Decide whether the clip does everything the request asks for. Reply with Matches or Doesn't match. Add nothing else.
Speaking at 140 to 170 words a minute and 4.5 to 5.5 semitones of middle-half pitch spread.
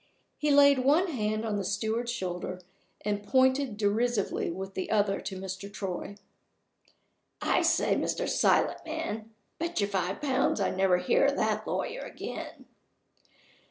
Matches